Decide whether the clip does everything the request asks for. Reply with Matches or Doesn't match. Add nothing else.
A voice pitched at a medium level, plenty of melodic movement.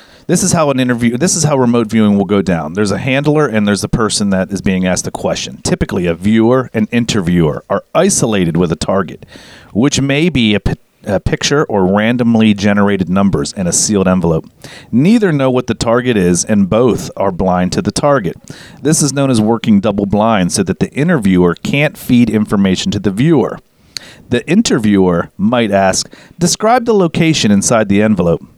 Doesn't match